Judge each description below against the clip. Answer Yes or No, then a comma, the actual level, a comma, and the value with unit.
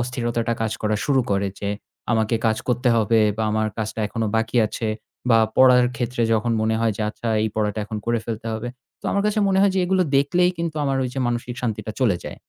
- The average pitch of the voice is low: Yes, low, 115 Hz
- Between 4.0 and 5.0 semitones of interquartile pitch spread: No, narrow, 2.6 semitones